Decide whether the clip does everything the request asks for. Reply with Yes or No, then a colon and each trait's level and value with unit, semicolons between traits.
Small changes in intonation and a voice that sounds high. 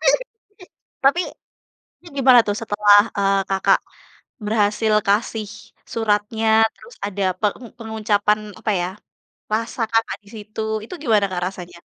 Yes: narrow, 1.8 semitones; high, 210 Hz